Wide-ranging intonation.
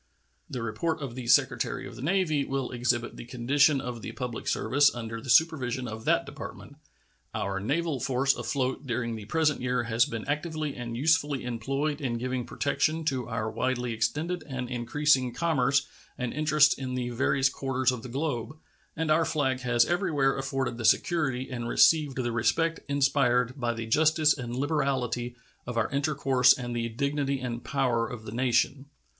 No: average, 3.2 semitones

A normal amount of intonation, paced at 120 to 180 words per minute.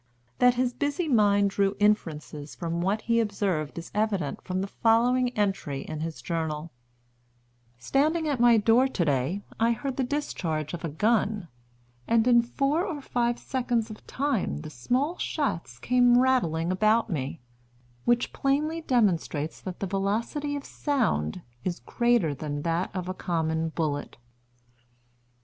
No: wide, 7.1 semitones; average, 150 wpm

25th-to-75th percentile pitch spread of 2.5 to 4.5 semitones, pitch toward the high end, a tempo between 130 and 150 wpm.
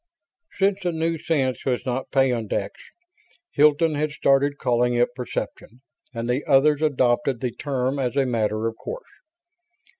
No: average, 3.5 semitones; low, 135 Hz; average, 145 wpm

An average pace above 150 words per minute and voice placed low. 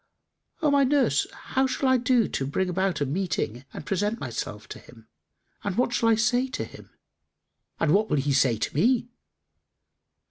No: average, 180 wpm; high, 195 Hz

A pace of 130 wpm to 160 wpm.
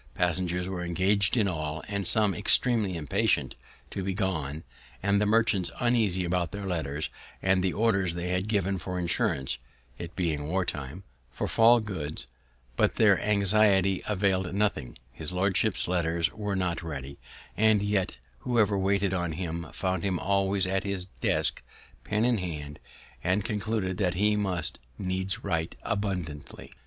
Yes: average, 150 wpm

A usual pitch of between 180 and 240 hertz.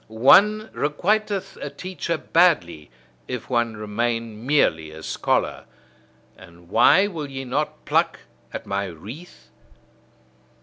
No: low, 125 Hz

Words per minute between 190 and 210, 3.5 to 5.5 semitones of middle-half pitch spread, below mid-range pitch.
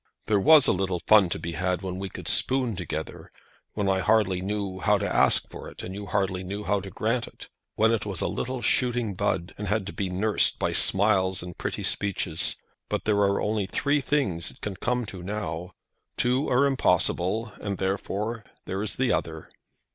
No: average, 200 wpm; average, 2.9 semitones; low, 100 Hz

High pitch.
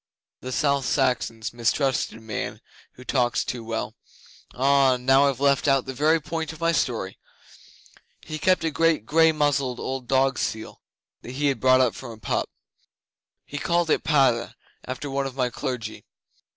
No: low, 135 Hz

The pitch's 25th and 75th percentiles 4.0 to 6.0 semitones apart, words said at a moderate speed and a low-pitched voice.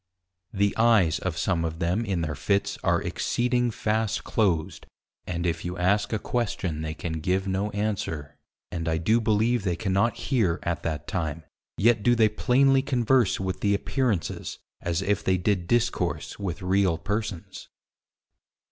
Yes: average, 4.4 semitones; average, 160 wpm; low, 100 Hz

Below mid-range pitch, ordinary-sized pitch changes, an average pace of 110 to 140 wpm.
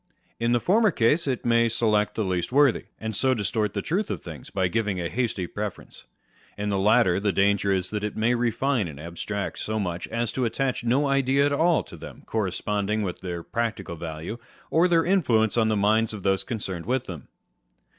No: low, 110 Hz; average, 4.0 semitones; fast, 205 wpm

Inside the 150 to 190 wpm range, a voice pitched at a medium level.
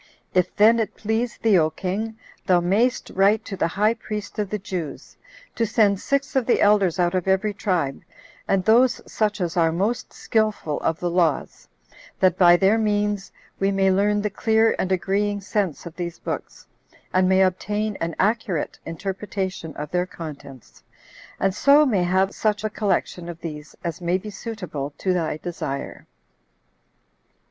No: average, 170 wpm; high, 195 Hz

